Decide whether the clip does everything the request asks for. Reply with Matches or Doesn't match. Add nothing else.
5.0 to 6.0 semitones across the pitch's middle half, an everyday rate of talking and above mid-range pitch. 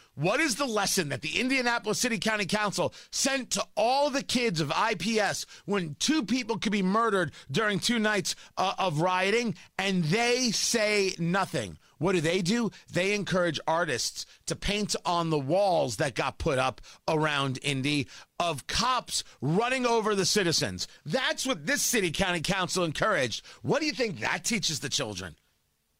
Matches